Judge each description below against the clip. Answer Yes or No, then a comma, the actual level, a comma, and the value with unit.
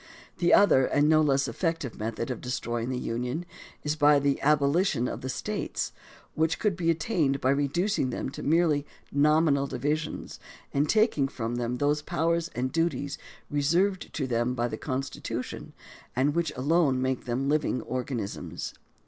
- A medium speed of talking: Yes, average, 155 wpm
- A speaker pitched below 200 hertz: Yes, medium, 140 Hz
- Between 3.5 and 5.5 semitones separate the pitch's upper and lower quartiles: Yes, average, 3.9 semitones